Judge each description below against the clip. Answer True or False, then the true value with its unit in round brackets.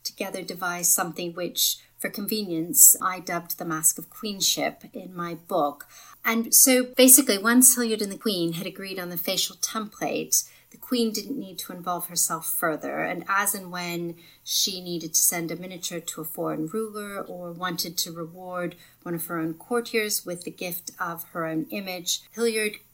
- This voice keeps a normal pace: True (180 wpm)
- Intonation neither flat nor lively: True (3.8 semitones)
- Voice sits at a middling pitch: True (180 Hz)